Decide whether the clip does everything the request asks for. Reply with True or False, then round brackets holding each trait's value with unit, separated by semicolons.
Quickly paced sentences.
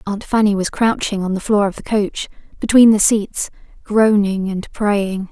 False (180 wpm)